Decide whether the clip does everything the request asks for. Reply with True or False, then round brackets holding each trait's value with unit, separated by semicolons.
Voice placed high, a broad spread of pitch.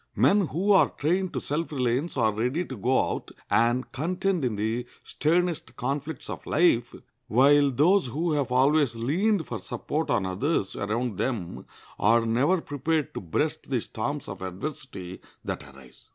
False (135 Hz; 5.7 semitones)